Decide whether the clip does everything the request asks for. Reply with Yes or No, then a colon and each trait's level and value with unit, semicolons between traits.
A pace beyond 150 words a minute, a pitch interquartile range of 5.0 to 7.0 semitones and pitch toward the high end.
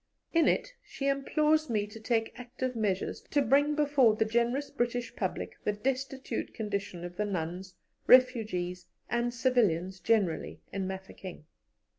No: average, 140 wpm; average, 5.3 semitones; high, 230 Hz